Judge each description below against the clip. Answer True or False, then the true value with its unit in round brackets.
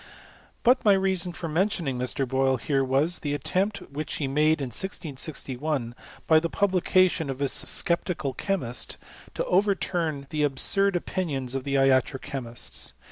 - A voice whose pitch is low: False (150 Hz)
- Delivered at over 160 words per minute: False (150 wpm)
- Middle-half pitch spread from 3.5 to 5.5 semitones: True (5.2 semitones)